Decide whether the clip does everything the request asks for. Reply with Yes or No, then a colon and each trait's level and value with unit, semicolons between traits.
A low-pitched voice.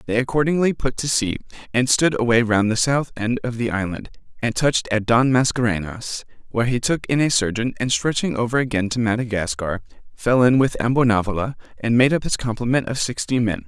Yes: low, 120 Hz